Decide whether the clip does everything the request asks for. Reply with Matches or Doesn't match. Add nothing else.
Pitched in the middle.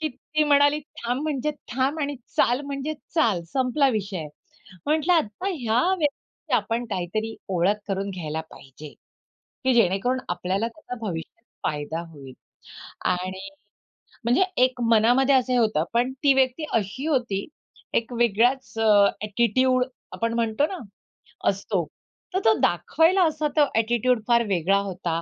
Doesn't match